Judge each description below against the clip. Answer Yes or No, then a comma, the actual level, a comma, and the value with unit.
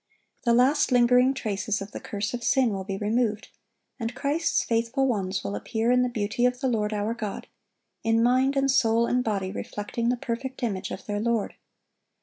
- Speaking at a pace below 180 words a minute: No, average, 190 wpm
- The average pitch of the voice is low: No, high, 230 Hz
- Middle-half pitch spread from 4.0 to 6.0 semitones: No, average, 3.2 semitones